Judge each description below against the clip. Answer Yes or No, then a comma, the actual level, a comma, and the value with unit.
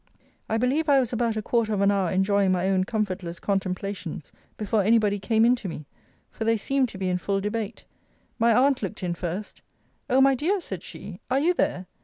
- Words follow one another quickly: Yes, fast, 215 wpm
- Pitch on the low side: No, high, 210 Hz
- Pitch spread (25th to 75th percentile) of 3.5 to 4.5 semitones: Yes, average, 3.8 semitones